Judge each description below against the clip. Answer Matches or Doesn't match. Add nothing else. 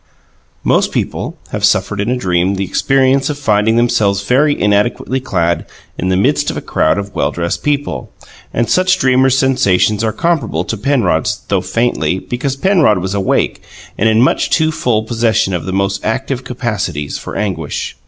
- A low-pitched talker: Matches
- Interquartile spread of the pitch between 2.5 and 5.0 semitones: Doesn't match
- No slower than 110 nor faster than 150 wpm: Doesn't match